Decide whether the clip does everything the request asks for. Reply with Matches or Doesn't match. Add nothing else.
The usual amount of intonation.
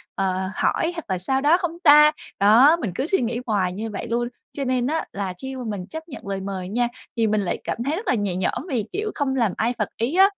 Doesn't match